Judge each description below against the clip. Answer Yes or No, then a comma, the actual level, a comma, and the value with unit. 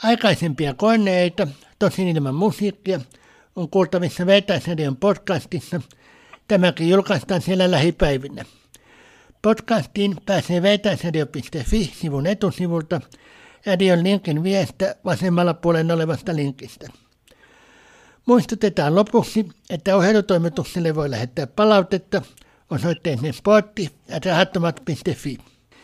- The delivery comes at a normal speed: No, slow, 85 wpm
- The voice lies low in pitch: No, medium, 180 Hz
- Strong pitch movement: No, average, 3.5 semitones